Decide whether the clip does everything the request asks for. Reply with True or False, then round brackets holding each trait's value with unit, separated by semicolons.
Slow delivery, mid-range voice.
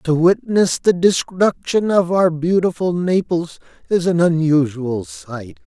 True (125 wpm; 170 Hz)